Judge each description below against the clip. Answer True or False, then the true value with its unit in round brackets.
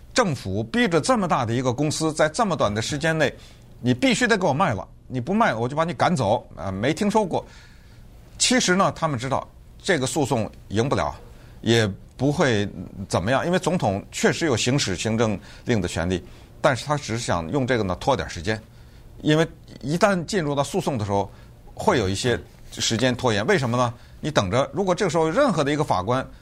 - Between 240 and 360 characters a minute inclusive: True (300 characters per minute)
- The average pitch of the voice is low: True (130 Hz)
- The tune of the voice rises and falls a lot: True (6.6 semitones)